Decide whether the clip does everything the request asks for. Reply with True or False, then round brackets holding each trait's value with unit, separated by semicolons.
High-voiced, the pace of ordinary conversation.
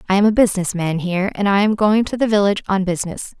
False (200 Hz; 265 wpm)